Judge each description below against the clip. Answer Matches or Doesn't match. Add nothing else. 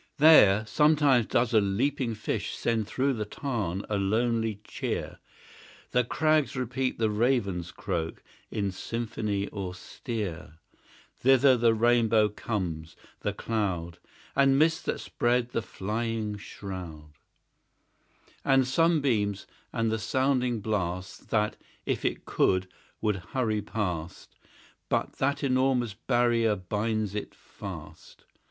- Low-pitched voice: Matches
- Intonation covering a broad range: Doesn't match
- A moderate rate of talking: Doesn't match